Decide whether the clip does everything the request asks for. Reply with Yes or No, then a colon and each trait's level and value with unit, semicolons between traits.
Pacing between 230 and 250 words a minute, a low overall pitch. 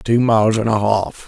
Yes: fast, 235 wpm; low, 110 Hz